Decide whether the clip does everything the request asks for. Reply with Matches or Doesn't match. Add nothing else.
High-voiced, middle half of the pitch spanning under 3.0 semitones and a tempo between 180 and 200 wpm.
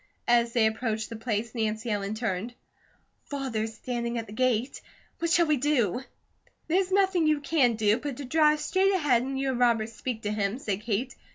Doesn't match